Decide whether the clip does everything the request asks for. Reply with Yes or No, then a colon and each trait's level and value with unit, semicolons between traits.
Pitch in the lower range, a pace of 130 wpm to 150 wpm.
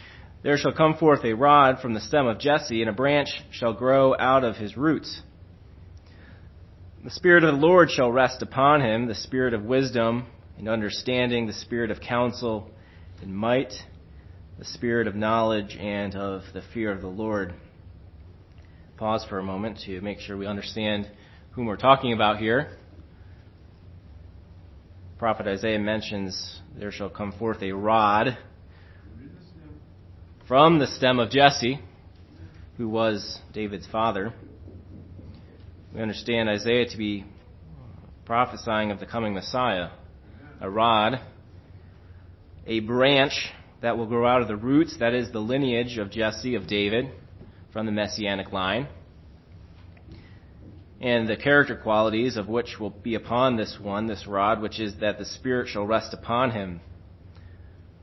Yes: low, 105 Hz; average, 145 wpm